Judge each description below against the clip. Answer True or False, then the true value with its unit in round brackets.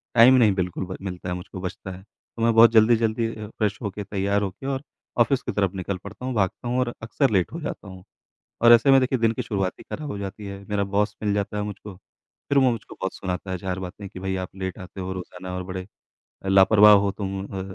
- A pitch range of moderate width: True (3.2 semitones)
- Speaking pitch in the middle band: False (100 Hz)